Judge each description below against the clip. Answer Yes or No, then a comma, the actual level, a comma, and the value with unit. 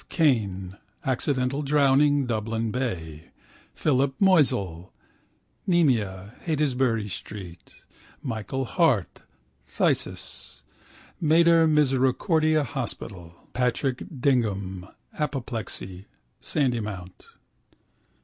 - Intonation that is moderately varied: No, wide, 6.2 semitones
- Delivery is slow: Yes, slow, 65 wpm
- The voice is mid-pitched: No, low, 125 Hz